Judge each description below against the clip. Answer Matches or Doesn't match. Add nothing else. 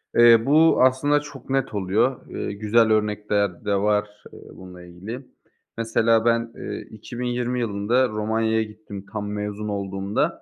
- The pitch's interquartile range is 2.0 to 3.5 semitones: Matches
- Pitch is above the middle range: Doesn't match